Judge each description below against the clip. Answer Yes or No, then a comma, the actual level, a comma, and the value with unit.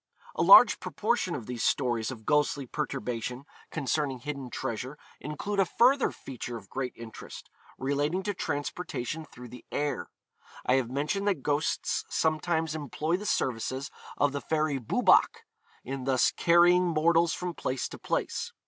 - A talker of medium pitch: Yes, medium, 145 Hz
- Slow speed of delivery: No, average, 150 wpm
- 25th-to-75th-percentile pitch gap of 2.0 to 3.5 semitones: No, average, 4.4 semitones